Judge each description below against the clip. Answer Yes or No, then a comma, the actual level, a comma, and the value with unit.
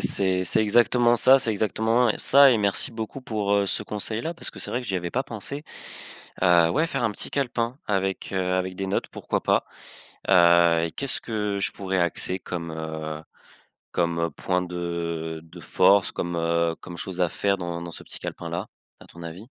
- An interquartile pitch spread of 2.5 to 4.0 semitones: No, average, 4.5 semitones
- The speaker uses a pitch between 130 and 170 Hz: No, very low, 95 Hz